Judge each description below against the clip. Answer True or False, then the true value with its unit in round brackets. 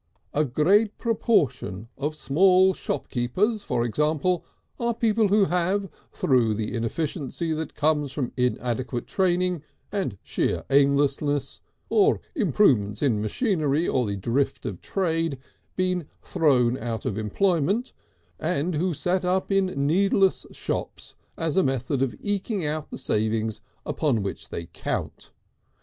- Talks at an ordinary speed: False (130 wpm)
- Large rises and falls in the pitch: True (6.8 semitones)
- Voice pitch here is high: False (155 Hz)